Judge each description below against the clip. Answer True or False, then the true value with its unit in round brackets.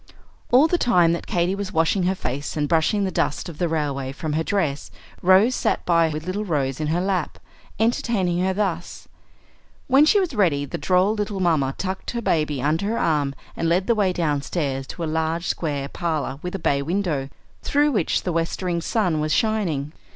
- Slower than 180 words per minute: False (200 wpm)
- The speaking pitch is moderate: True (170 Hz)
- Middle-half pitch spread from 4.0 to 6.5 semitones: True (4.3 semitones)